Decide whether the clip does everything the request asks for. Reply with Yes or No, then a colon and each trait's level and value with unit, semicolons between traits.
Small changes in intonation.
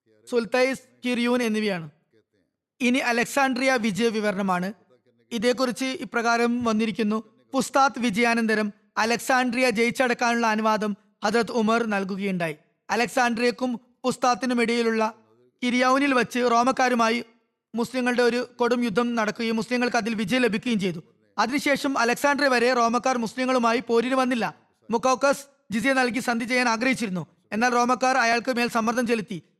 Yes: narrow, 2.3 semitones